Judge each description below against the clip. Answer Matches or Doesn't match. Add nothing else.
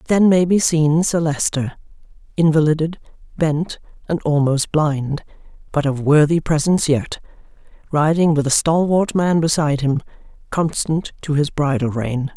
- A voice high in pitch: Doesn't match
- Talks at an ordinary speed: Doesn't match